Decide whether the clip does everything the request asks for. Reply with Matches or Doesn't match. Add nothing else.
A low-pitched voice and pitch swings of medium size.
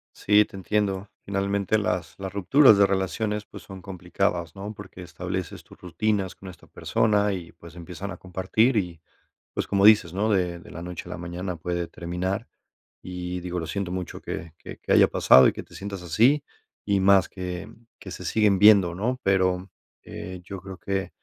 Doesn't match